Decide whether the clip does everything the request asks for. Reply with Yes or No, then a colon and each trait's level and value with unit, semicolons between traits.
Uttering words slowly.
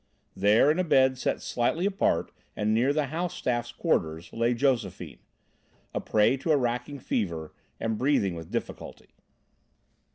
No: average, 150 wpm